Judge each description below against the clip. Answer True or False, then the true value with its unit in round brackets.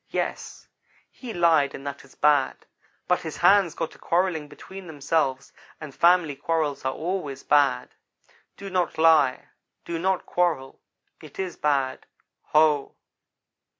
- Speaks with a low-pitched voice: False (155 Hz)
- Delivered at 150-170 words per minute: False (135 wpm)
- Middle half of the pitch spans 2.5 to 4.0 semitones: True (3.6 semitones)